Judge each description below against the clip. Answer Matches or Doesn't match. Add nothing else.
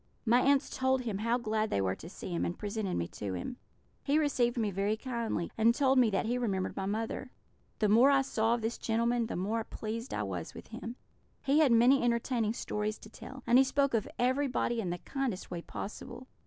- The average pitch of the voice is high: Matches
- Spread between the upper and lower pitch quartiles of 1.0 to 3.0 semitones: Doesn't match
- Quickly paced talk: Matches